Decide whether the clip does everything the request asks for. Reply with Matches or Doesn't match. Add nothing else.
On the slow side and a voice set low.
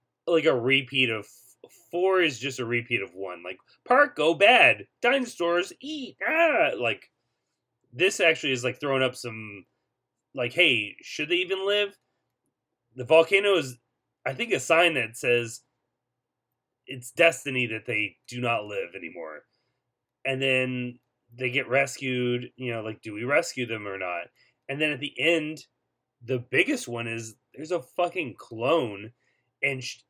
Doesn't match